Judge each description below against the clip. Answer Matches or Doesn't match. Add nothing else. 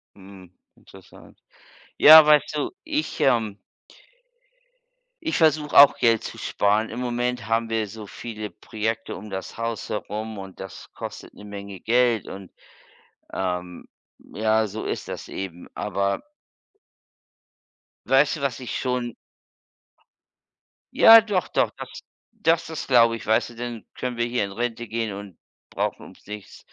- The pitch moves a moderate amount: Matches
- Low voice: Matches